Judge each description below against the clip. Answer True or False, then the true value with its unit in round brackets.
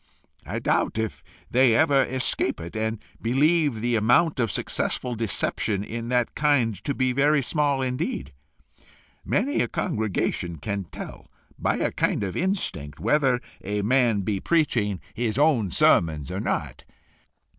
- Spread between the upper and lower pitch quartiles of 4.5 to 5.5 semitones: True (5.0 semitones)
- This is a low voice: True (120 Hz)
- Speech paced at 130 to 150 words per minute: True (145 wpm)